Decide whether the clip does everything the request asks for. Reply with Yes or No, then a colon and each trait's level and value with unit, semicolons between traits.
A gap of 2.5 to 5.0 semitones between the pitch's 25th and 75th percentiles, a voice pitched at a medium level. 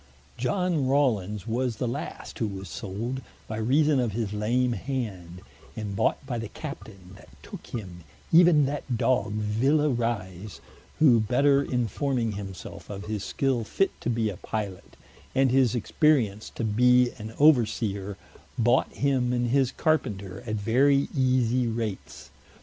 No: average, 4.0 semitones; low, 120 Hz